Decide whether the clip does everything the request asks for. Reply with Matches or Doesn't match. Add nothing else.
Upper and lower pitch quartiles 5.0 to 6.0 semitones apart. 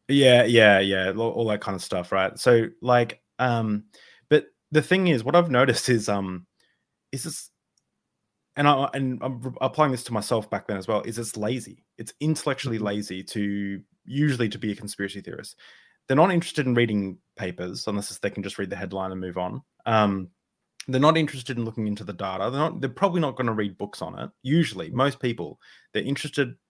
Matches